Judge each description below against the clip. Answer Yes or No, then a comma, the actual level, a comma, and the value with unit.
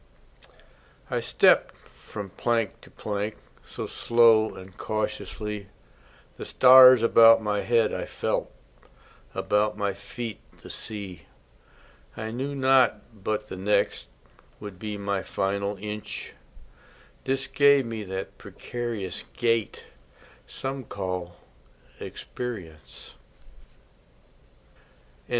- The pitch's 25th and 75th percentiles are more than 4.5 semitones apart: No, average, 2.8 semitones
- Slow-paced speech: Yes, slow, 100 wpm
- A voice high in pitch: No, low, 105 Hz